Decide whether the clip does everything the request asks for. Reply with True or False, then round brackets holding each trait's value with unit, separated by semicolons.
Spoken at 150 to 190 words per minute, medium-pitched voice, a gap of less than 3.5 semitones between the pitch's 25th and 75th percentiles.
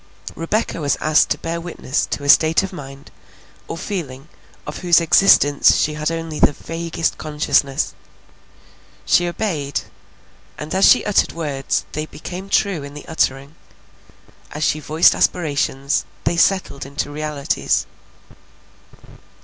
False (135 wpm; 155 Hz; 2.9 semitones)